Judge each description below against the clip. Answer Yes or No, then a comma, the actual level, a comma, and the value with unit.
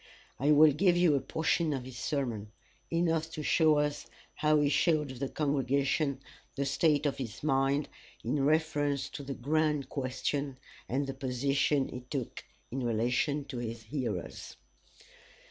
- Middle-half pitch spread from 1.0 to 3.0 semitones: Yes, narrow, 2.5 semitones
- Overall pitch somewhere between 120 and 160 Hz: Yes, medium, 140 Hz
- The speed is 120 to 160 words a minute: Yes, average, 145 wpm